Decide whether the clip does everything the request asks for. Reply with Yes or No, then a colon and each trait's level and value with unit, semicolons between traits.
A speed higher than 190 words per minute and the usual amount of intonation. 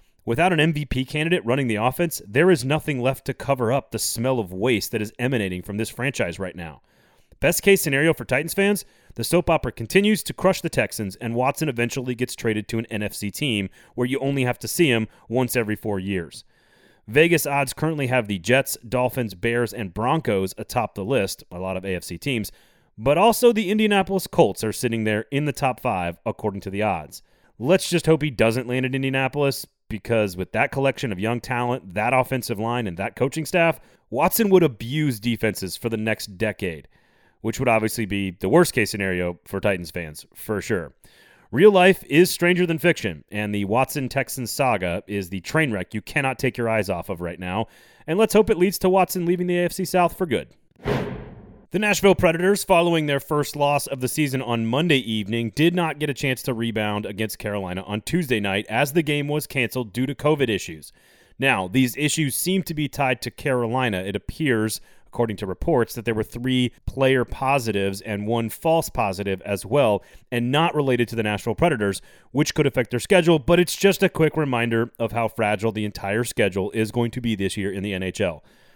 No: fast, 205 wpm; wide, 5.9 semitones